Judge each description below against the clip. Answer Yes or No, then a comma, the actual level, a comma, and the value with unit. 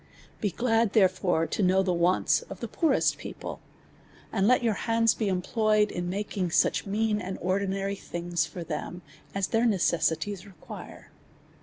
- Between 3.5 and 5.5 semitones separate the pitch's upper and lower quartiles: No, average, 3.1 semitones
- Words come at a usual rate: Yes, average, 160 wpm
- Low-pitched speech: No, high, 195 Hz